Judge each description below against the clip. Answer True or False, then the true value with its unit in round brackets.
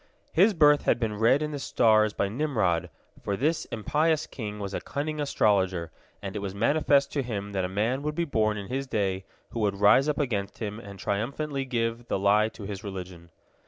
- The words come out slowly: False (205 wpm)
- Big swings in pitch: True (5.8 semitones)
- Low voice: True (110 Hz)